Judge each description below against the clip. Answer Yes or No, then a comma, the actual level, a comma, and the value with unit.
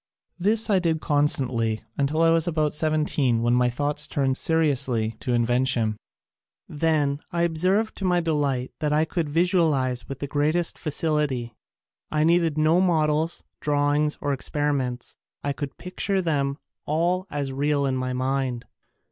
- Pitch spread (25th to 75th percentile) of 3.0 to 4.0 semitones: Yes, average, 3.5 semitones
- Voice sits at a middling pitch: Yes, medium, 150 Hz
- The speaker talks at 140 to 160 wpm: Yes, average, 155 wpm